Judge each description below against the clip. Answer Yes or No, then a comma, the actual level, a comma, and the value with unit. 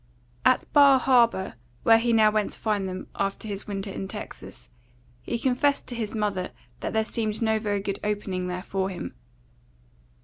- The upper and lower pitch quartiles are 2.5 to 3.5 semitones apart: Yes, average, 2.8 semitones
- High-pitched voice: Yes, high, 210 Hz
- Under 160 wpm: No, average, 175 wpm